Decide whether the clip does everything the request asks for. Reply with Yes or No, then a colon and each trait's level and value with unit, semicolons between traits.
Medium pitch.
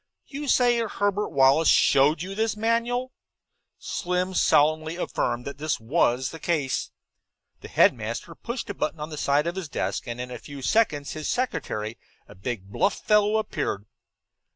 Yes: medium, 155 Hz